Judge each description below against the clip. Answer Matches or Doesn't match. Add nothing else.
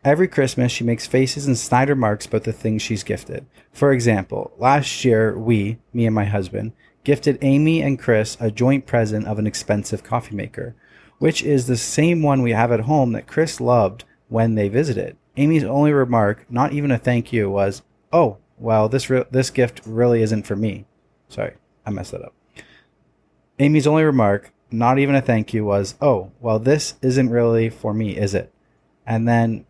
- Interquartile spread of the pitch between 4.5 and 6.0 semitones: Doesn't match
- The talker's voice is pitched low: Matches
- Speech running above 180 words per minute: Matches